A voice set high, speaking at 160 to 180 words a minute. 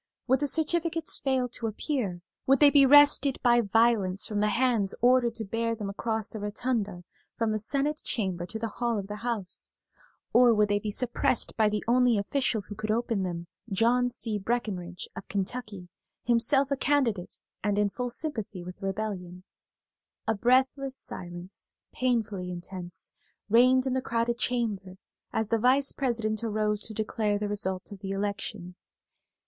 Yes: high, 220 Hz; average, 165 wpm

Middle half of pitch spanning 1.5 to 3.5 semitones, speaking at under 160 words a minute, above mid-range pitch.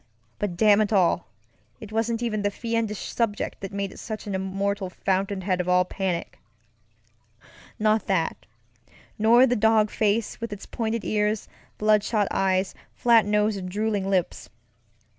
Yes: narrow, 2.6 semitones; average, 145 wpm; high, 205 Hz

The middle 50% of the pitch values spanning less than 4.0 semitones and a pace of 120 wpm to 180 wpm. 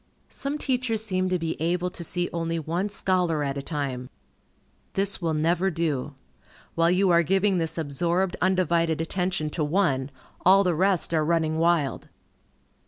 Yes: average, 2.8 semitones; average, 160 wpm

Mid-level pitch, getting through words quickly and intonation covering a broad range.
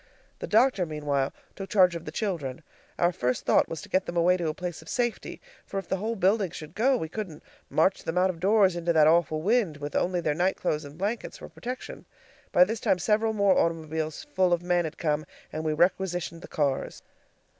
No: medium, 175 Hz; fast, 220 wpm; average, 3.6 semitones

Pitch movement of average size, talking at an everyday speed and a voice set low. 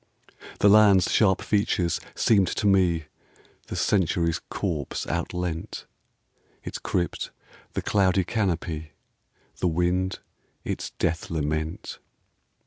No: average, 3.0 semitones; slow, 100 wpm; very low, 90 Hz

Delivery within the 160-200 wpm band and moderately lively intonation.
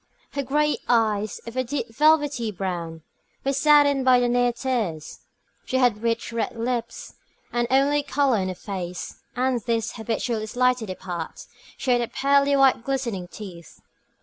No: average, 145 wpm; average, 4.0 semitones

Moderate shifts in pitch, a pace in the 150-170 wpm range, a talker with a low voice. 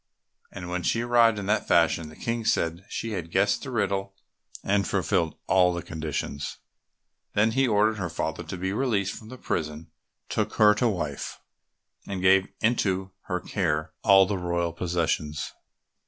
Yes: average, 3.9 semitones; average, 165 wpm; very low, 95 Hz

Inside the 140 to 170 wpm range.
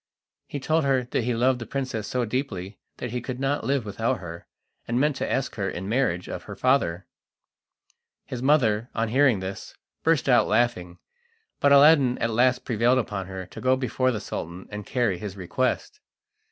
No: average, 180 wpm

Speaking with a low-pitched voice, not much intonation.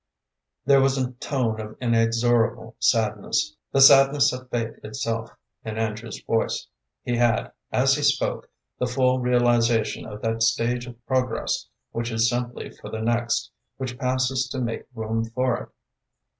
Yes: low, 120 Hz; narrow, 2.1 semitones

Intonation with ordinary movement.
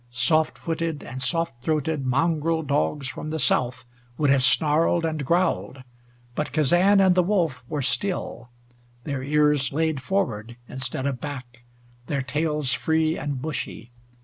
Yes: average, 3.6 semitones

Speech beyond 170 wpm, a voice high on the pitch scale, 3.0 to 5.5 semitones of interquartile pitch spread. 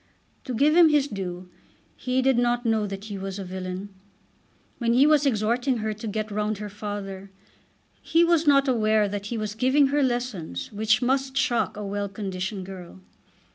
Yes: average, 180 wpm; high, 215 Hz; average, 4.6 semitones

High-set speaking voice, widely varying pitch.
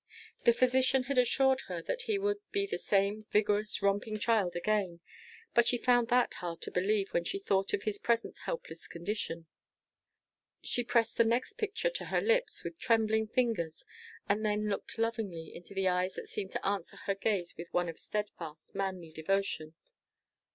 No: high, 210 Hz; average, 4.4 semitones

